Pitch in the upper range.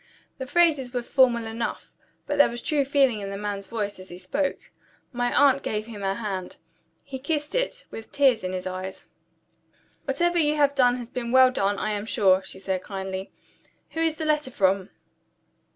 Yes: high, 235 Hz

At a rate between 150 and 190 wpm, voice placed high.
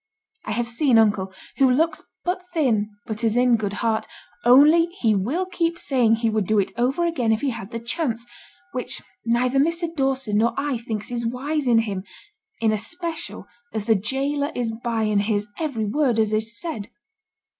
Yes: average, 185 wpm; high, 235 Hz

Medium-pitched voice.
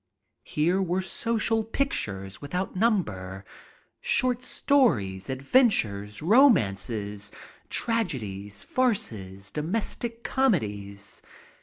Yes: medium, 150 Hz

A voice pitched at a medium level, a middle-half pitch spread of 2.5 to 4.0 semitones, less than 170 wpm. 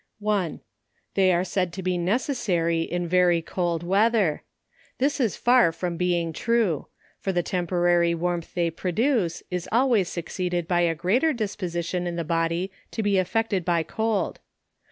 Yes: medium, 180 Hz; average, 3.4 semitones; average, 160 wpm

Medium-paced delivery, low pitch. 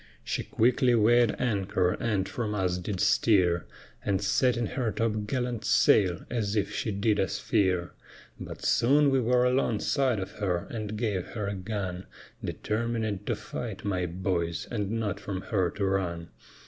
Yes: average, 160 wpm; low, 105 Hz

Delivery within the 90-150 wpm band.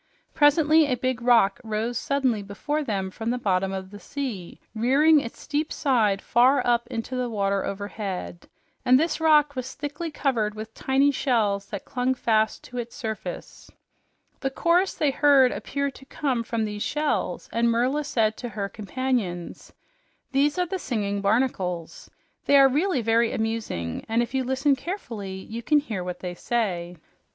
No: average, 165 wpm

